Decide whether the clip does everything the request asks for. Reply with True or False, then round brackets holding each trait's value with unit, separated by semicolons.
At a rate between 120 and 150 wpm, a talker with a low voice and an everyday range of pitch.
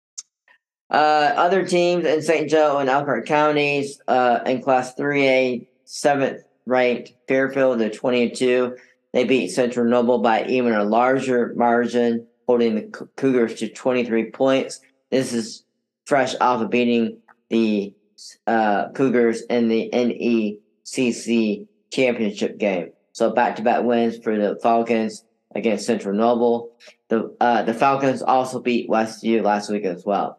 False (140 wpm; 120 Hz; 2.3 semitones)